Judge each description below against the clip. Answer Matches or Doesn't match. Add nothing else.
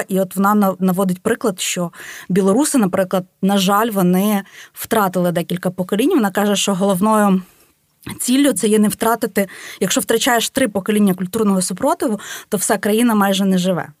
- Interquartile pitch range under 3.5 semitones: Matches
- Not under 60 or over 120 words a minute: Doesn't match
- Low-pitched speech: Doesn't match